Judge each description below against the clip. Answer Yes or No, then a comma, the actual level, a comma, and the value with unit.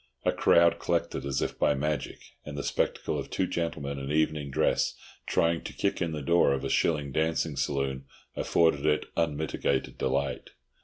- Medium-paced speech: Yes, average, 170 wpm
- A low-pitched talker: Yes, very low, 75 Hz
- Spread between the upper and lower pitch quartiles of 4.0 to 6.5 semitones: No, average, 2.7 semitones